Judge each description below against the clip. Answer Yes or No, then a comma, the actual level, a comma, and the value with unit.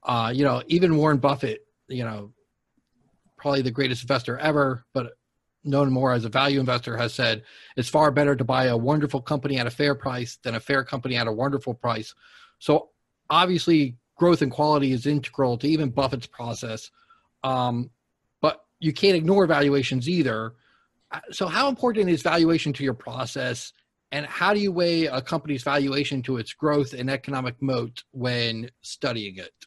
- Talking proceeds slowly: No, average, 170 wpm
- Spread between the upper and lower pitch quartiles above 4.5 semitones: No, average, 3.2 semitones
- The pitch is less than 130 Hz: No, low, 135 Hz